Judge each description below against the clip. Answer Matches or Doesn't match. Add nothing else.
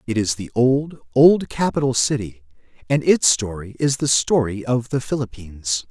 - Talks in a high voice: Doesn't match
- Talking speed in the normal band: Matches